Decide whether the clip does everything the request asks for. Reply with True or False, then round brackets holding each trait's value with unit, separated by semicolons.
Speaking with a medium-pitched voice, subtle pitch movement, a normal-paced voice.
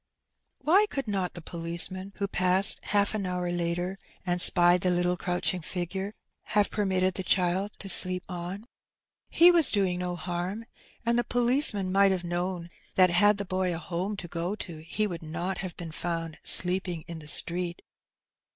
True (180 Hz; 2.2 semitones; 185 wpm)